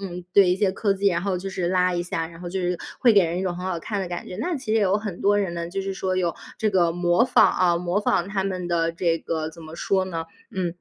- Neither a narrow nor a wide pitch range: No, narrow, 2.1 semitones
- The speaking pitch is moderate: Yes, medium, 180 Hz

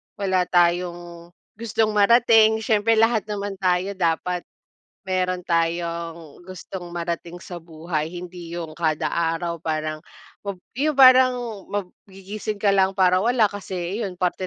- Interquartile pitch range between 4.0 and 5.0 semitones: No, average, 3.1 semitones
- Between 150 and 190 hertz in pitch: Yes, medium, 185 Hz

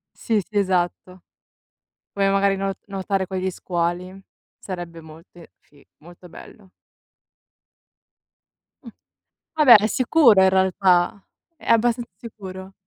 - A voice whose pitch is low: No, high, 190 Hz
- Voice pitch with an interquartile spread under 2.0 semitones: No, narrow, 2.5 semitones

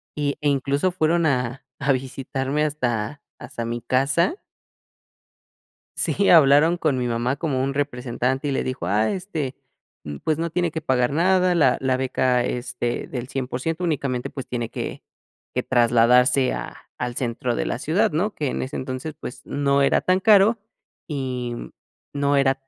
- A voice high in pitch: No, low, 135 Hz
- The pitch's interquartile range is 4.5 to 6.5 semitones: No, average, 3.6 semitones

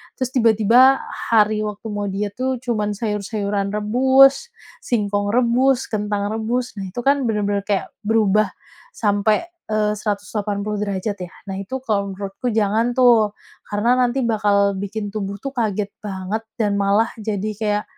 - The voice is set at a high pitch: Yes, high, 210 Hz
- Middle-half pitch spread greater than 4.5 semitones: No, narrow, 2.5 semitones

